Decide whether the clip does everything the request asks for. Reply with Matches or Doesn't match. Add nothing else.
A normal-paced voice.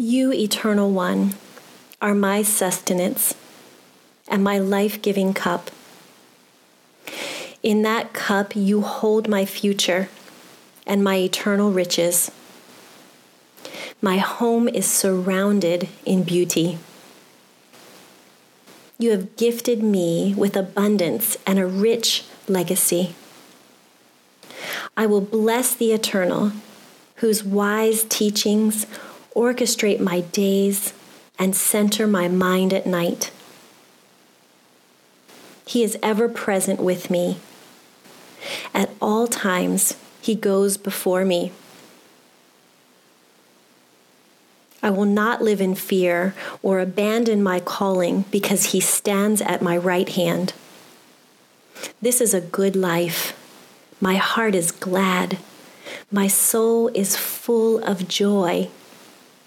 Doesn't match